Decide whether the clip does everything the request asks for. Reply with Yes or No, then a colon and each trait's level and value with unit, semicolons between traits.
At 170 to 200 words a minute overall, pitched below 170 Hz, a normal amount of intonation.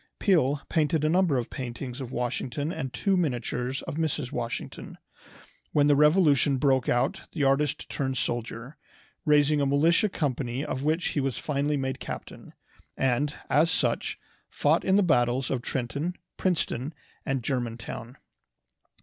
No: average, 145 wpm; medium, 140 Hz; average, 3.4 semitones